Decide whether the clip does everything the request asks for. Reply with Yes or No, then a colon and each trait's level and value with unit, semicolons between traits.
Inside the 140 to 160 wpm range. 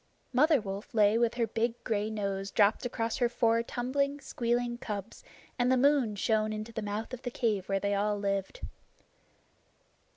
No: average, 170 wpm